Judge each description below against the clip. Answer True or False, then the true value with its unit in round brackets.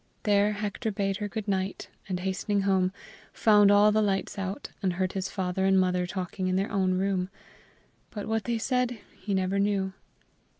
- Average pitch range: False (1.8 semitones)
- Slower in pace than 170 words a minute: False (175 wpm)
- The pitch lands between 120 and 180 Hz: False (195 Hz)